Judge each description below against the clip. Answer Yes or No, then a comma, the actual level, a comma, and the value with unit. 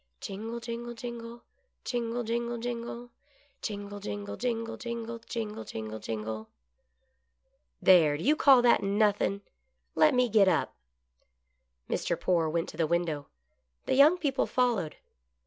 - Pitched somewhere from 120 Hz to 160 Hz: No, high, 225 Hz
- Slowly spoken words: Yes, slow, 130 wpm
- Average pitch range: No, wide, 5.7 semitones